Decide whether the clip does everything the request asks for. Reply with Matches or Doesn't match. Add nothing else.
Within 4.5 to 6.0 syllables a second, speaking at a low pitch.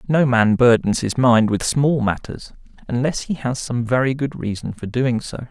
Matches